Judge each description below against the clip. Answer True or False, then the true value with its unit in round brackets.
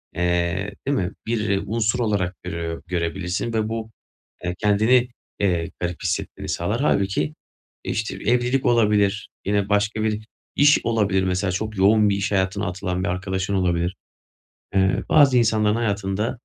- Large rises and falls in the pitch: False (3.0 semitones)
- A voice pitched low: True (100 Hz)